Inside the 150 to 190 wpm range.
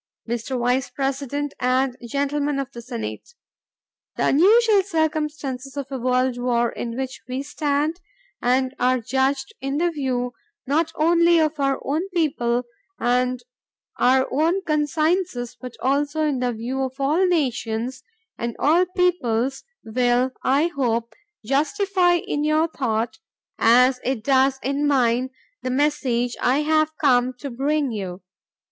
No: slow, 135 wpm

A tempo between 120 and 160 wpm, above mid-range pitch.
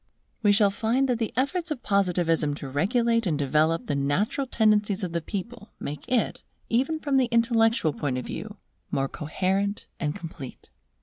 No: average, 170 wpm; high, 205 Hz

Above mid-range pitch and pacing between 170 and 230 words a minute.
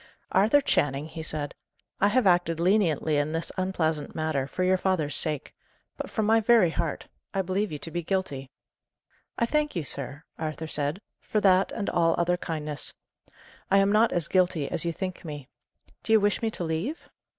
No: medium, 175 Hz; average, 185 wpm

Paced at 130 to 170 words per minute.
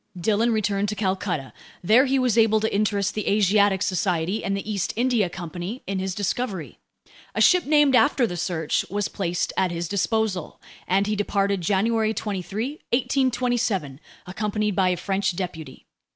Yes: average, 165 wpm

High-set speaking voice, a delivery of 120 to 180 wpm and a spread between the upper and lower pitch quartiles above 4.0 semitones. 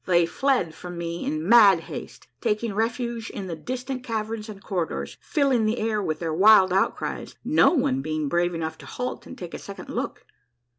No: high, 200 Hz; average, 195 wpm; average, 5.3 semitones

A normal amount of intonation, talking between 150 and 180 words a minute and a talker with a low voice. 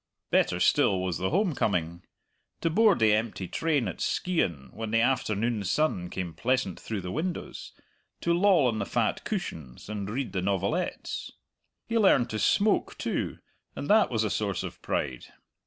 No: wide, 8.8 semitones; average, 170 wpm; low, 110 Hz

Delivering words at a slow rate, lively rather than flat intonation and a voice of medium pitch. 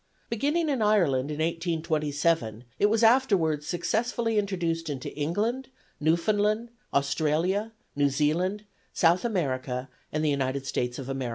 Yes: slow, 125 wpm; wide, 6.6 semitones; medium, 165 Hz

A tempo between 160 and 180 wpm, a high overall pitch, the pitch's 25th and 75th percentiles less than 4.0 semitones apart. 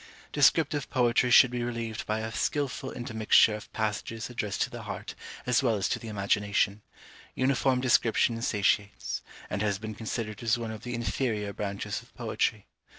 No: average, 165 wpm; low, 115 Hz; narrow, 2.5 semitones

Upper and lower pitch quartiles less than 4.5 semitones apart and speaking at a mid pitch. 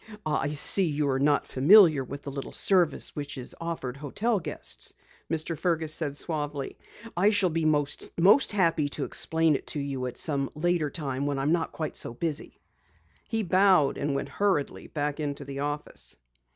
Yes: average, 3.1 semitones; medium, 150 Hz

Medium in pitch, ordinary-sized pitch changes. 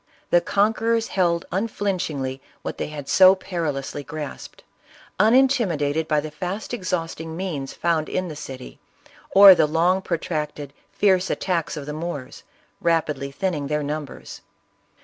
Yes: medium, 165 Hz; average, 4.1 semitones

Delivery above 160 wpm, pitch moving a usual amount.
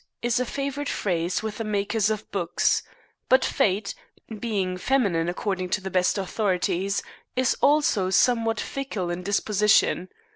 No: average, 140 wpm; average, 4.1 semitones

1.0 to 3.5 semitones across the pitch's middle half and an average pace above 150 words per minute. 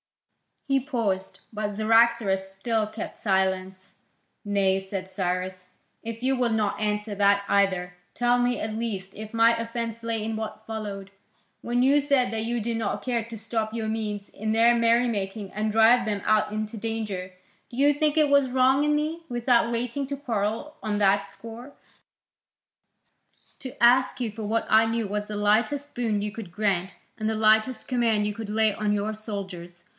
Yes: narrow, 2.6 semitones; average, 180 wpm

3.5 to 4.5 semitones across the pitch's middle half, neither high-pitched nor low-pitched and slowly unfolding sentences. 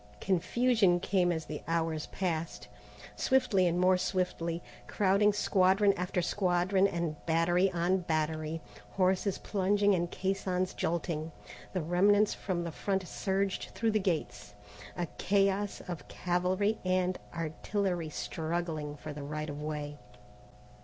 No: average, 2.9 semitones; medium, 180 Hz; slow, 125 wpm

